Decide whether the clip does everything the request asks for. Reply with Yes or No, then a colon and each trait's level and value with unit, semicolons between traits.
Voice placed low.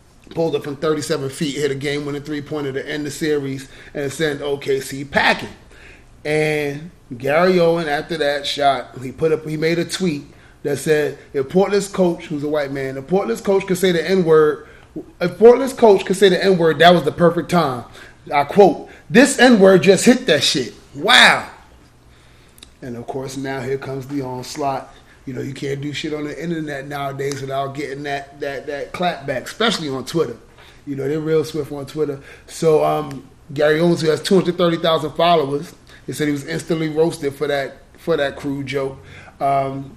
No: medium, 150 Hz